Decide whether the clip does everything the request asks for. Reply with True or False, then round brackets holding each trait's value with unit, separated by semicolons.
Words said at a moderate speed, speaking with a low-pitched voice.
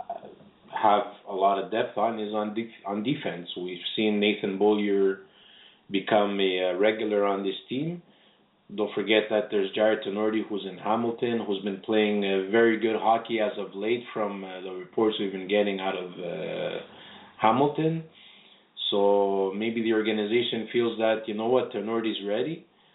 True (165 wpm; 105 Hz)